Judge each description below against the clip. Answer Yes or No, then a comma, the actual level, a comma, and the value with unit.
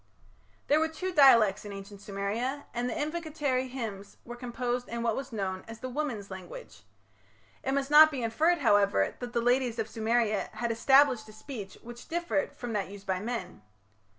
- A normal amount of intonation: Yes, average, 4.6 semitones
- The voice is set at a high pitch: Yes, high, 240 Hz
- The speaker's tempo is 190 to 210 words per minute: No, average, 180 wpm